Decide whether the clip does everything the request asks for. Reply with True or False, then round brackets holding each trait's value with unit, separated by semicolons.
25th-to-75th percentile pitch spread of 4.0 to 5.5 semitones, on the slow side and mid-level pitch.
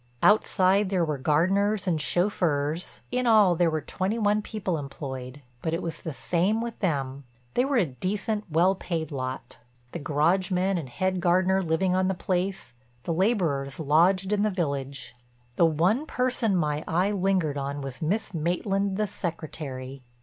False (4.7 semitones; 160 wpm; 175 Hz)